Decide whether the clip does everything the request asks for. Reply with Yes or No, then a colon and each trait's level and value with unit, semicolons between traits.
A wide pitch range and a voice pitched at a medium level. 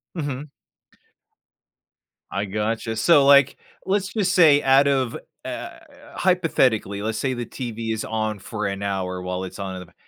No: wide, 5.9 semitones; low, 115 Hz